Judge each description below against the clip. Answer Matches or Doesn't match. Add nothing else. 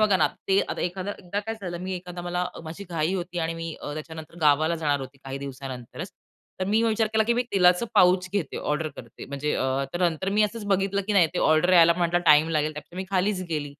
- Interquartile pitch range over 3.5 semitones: Matches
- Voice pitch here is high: Doesn't match